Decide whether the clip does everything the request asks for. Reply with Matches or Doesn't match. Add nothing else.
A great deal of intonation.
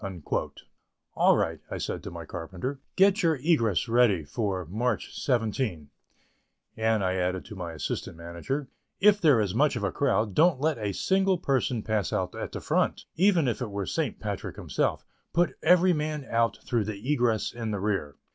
Matches